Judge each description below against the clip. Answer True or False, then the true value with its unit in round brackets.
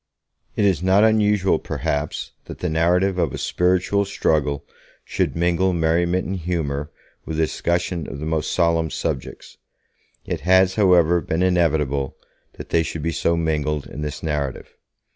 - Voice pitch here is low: True (85 Hz)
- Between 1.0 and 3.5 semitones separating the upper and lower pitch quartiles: True (3.0 semitones)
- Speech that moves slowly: False (155 wpm)